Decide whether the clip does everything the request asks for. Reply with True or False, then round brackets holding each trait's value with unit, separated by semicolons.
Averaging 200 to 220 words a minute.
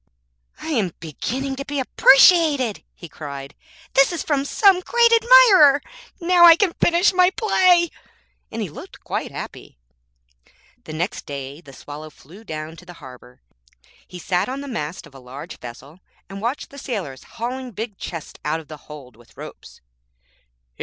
False (165 wpm)